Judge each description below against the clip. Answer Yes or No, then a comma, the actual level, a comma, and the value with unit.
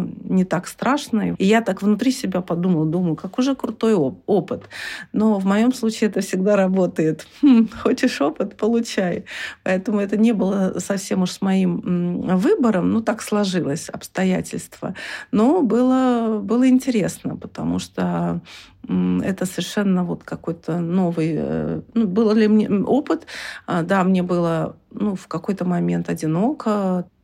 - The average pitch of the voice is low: No, high, 195 Hz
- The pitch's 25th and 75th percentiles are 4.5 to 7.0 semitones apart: No, average, 4.1 semitones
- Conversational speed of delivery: Yes, average, 140 wpm